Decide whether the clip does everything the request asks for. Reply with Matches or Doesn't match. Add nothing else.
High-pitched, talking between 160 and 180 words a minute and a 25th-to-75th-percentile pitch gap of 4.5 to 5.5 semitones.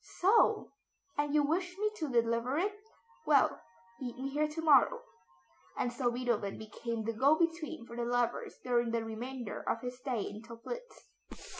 Matches